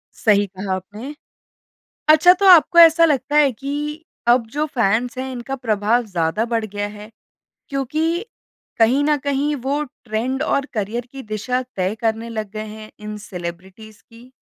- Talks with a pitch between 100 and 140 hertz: No, high, 235 Hz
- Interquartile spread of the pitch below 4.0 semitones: No, average, 4.6 semitones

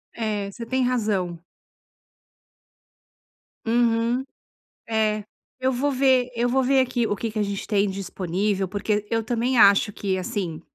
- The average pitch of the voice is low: No, high, 220 Hz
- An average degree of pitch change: Yes, average, 3.5 semitones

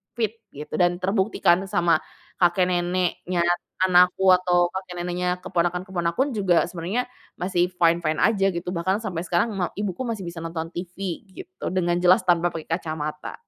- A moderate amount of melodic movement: No, narrow, 1.7 semitones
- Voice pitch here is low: No, medium, 180 Hz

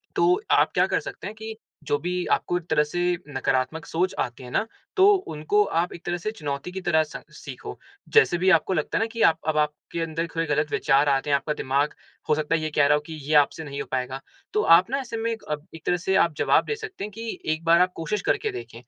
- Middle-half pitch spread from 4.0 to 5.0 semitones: Yes, average, 4.5 semitones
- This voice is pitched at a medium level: Yes, medium, 165 Hz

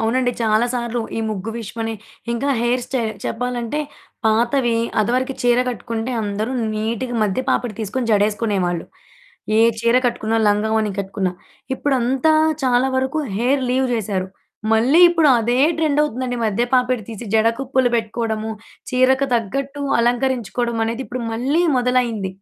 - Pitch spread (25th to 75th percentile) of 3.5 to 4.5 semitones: No, average, 2.7 semitones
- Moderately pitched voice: No, high, 235 Hz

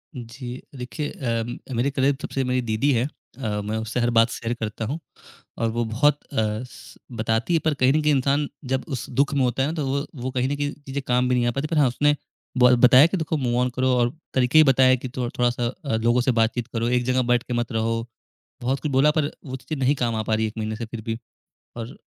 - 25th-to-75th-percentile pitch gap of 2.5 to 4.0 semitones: Yes, average, 2.9 semitones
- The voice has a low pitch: Yes, low, 125 Hz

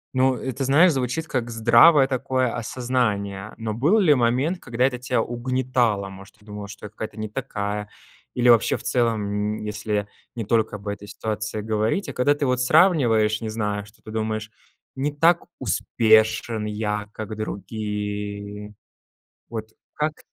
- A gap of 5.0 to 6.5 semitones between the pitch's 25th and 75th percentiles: No, average, 3.5 semitones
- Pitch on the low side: Yes, low, 110 Hz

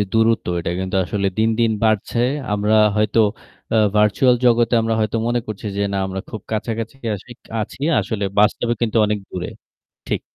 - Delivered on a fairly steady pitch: Yes, narrow, 1.8 semitones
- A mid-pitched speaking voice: No, low, 110 Hz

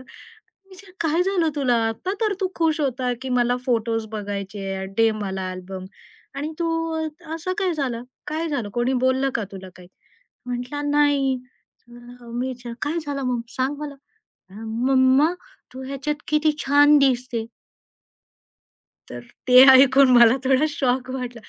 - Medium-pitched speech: No, very high, 260 Hz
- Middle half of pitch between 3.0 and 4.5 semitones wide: Yes, average, 3.8 semitones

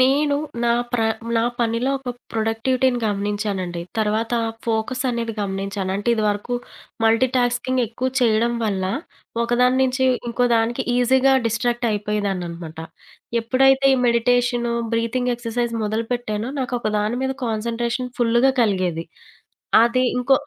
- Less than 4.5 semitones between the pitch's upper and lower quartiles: Yes, narrow, 2.6 semitones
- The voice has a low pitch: No, high, 235 Hz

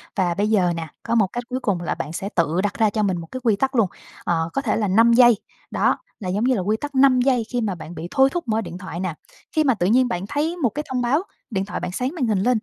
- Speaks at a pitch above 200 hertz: Yes, high, 220 Hz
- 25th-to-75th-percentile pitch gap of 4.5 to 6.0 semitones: Yes, average, 5.3 semitones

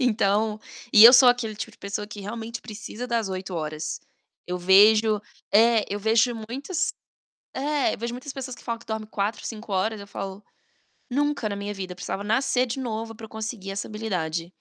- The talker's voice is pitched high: Yes, high, 220 Hz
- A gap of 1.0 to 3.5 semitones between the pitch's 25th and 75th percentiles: Yes, average, 2.8 semitones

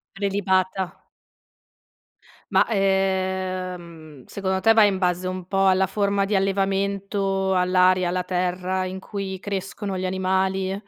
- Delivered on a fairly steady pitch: Yes, narrow, 1.1 semitones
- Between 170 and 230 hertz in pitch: Yes, high, 190 Hz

